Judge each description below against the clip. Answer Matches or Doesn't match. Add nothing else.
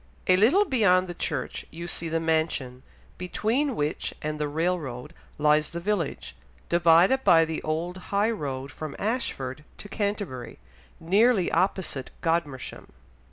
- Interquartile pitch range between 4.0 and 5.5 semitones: Matches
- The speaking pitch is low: Doesn't match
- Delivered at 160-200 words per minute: Doesn't match